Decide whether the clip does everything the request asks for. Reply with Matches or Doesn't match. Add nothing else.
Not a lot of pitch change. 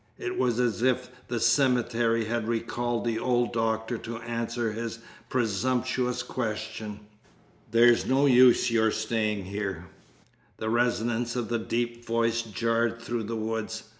Matches